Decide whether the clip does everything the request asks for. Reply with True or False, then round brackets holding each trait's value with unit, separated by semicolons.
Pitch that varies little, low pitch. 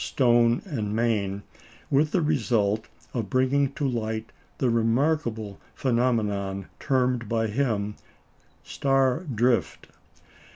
False (3.6 semitones; 120 Hz)